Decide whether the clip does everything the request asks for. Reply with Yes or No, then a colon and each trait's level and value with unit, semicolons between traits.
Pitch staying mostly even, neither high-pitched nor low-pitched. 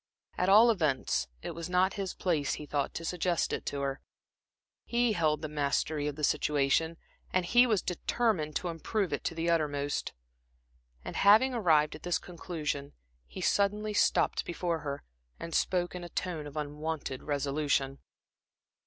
No: average, 3.9 semitones; medium, 165 Hz